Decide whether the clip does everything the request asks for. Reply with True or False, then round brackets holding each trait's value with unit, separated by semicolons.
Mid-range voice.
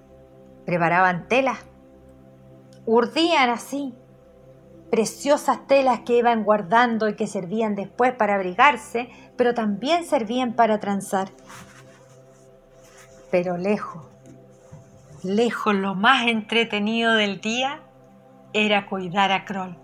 False (210 Hz)